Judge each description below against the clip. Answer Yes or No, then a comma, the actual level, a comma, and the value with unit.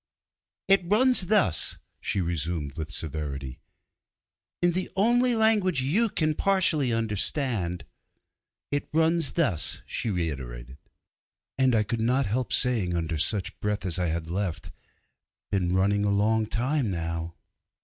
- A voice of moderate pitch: No, low, 105 Hz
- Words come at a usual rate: No, slow, 130 wpm